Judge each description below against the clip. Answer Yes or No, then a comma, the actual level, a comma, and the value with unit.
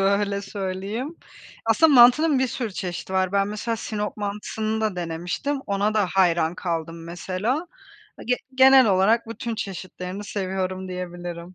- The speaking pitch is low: No, high, 200 Hz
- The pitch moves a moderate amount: Yes, average, 3.6 semitones